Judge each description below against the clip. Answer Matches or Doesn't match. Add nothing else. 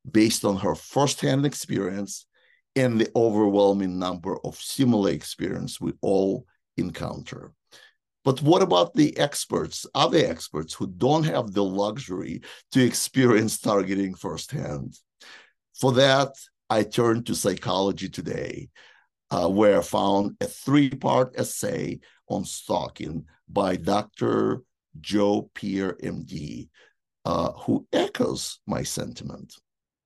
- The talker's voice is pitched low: Matches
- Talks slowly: Matches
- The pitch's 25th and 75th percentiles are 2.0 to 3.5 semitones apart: Doesn't match